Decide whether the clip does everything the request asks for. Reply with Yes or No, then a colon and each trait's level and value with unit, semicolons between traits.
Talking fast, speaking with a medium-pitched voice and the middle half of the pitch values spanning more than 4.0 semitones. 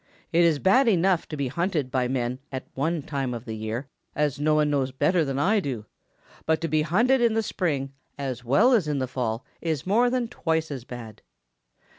Yes: fast, 210 wpm; medium, 150 Hz; average, 5.1 semitones